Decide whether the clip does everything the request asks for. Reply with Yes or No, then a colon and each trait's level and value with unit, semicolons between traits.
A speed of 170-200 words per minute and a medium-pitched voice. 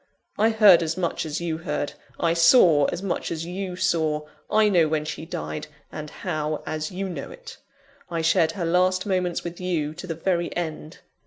Yes: average, 195 wpm; medium, 170 Hz